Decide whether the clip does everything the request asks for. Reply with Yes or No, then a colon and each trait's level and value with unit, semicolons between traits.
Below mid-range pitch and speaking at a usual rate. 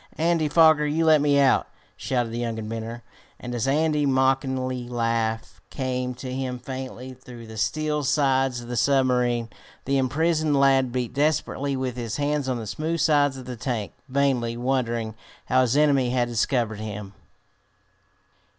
Yes: low, 130 Hz; average, 160 wpm